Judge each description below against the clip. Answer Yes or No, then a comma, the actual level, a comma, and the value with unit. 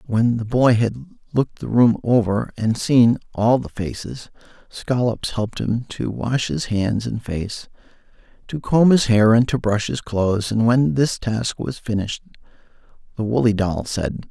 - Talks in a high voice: No, low, 115 Hz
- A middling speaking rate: Yes, average, 170 wpm